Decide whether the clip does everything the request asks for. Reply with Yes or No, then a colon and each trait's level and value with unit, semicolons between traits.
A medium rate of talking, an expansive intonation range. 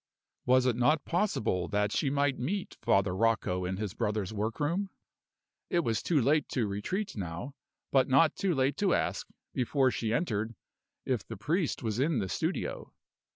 Yes: average, 170 wpm; wide, 6.1 semitones